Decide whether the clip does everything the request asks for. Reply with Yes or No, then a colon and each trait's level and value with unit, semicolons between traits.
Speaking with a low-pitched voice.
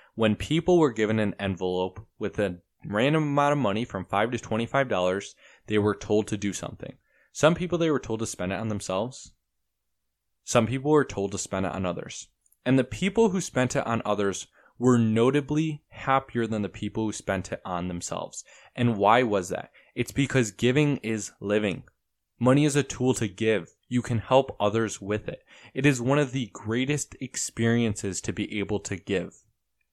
Yes: low, 110 Hz